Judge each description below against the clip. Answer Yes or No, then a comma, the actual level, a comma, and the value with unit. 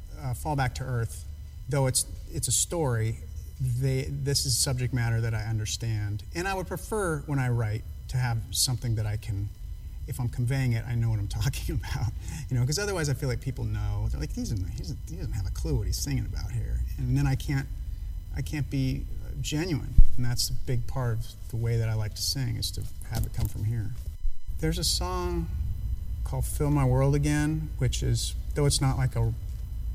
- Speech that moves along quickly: Yes, fast, 215 wpm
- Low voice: Yes, low, 115 Hz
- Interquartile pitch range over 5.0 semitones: Yes, wide, 5.5 semitones